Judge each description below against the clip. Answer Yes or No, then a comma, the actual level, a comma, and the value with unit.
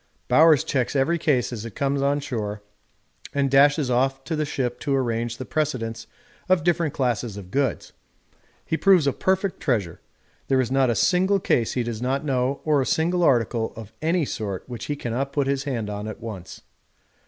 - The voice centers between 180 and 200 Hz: No, low, 135 Hz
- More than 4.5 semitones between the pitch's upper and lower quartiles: No, average, 4.1 semitones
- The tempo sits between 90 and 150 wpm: No, average, 190 wpm